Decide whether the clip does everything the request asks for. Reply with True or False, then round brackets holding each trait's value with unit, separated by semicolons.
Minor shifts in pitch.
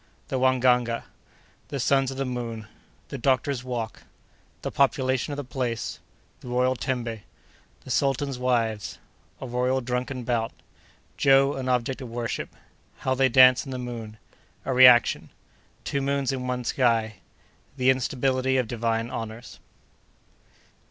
True (2.0 semitones)